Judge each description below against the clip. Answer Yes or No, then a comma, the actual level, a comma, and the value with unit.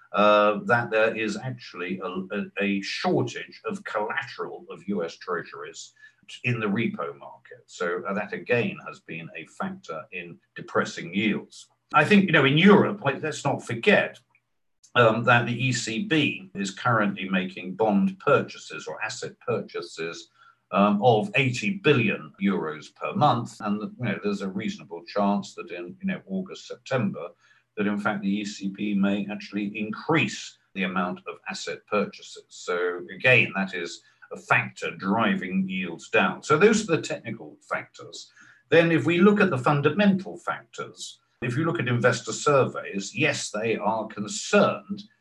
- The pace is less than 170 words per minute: Yes, average, 155 wpm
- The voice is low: Yes, low, 130 Hz